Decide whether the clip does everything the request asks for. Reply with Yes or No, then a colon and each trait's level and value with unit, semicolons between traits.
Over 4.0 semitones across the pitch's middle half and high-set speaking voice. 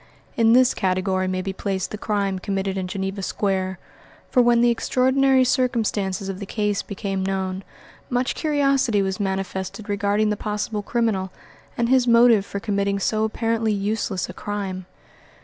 No: average, 3.2 semitones; high, 205 Hz